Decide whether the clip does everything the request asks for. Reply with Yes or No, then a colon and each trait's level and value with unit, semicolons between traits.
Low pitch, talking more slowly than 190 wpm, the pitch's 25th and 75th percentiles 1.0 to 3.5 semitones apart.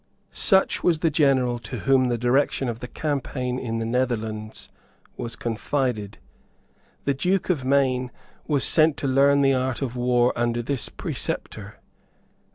Yes: low, 130 Hz; average, 150 wpm; average, 2.7 semitones